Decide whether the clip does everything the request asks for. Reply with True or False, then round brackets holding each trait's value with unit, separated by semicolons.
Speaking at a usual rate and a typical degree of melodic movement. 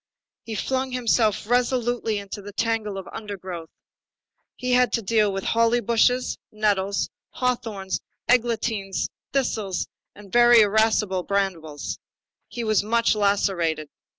False (120 wpm; 3.4 semitones)